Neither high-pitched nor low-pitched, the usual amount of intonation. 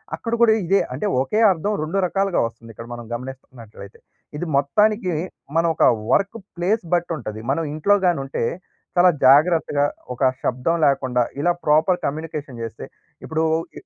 No: medium, 155 Hz; wide, 5.8 semitones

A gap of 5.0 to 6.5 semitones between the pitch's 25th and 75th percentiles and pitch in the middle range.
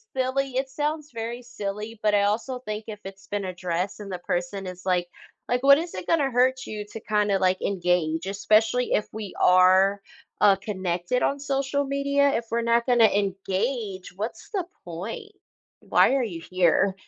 No: average, 5.3 semitones; high, 210 Hz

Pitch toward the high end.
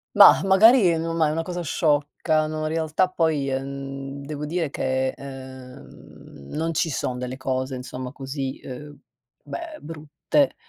No: medium, 145 Hz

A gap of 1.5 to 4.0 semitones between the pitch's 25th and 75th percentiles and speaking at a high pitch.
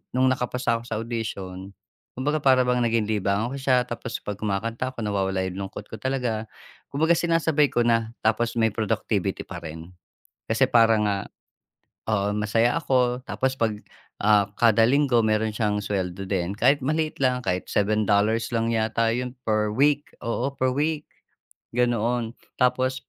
No: average, 3.5 semitones; low, 115 Hz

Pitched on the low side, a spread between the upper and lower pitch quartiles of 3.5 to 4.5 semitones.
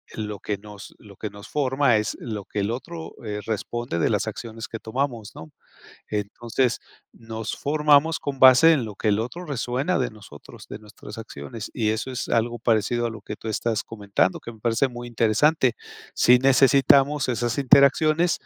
Yes: low, 115 Hz; average, 4.0 semitones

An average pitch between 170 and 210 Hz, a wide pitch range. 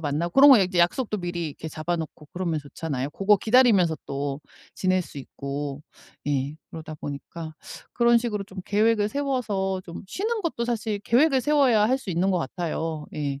Yes: medium, 185 Hz; wide, 6.7 semitones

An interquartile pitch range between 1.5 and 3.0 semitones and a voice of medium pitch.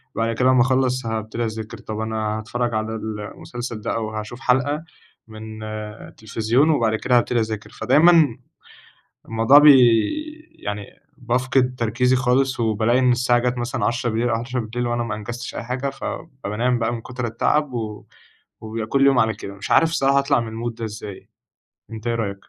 No: narrow, 2.5 semitones; low, 120 Hz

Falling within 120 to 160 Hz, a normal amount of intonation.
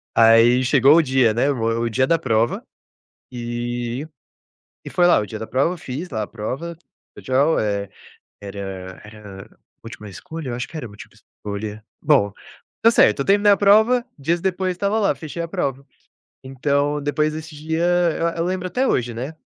No: low, 135 Hz; wide, 6.7 semitones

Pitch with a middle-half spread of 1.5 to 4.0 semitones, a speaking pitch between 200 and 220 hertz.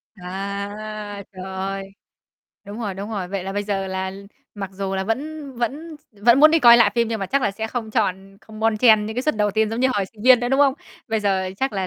Yes: average, 3.4 semitones; high, 210 Hz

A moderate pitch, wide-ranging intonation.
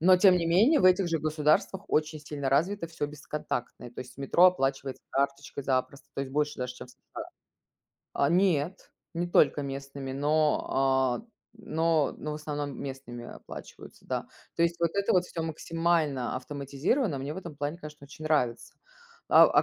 No: medium, 150 Hz; average, 3.6 semitones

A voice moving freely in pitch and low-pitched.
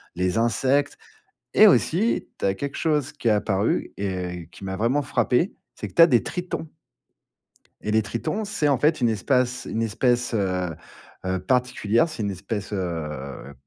Yes: wide, 6.8 semitones; low, 115 Hz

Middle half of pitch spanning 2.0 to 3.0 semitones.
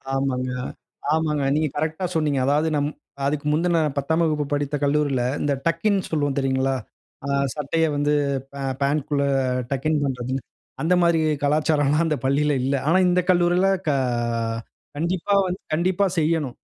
Yes: narrow, 2.6 semitones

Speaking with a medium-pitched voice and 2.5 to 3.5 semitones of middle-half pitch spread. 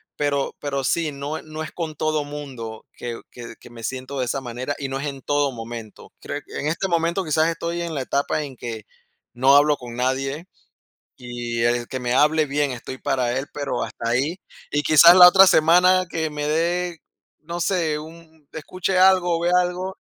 No: medium, 145 Hz; average, 4.3 semitones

